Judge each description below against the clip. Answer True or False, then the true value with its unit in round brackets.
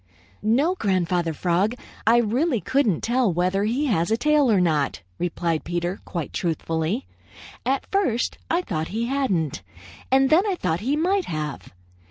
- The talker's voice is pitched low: False (210 Hz)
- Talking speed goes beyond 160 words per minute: False (155 wpm)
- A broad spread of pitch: True (7.8 semitones)